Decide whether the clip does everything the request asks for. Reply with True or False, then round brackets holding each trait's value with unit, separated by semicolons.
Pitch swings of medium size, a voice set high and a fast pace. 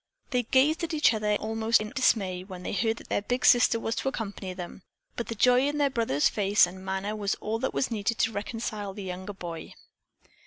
True (3.8 semitones; 215 Hz; 220 wpm)